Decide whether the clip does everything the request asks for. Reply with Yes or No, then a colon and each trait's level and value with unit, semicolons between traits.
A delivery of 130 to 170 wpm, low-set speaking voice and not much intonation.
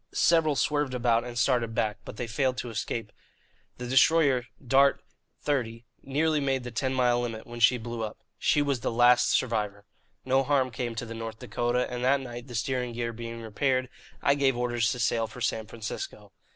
No: average, 190 wpm; low, 120 Hz; narrow, 2.3 semitones